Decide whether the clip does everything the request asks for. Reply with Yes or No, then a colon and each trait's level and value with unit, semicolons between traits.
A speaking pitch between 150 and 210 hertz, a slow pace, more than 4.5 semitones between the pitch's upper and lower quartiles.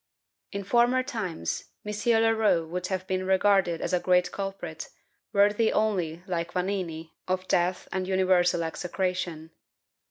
No: medium, 185 Hz; slow, 130 wpm; narrow, 2.5 semitones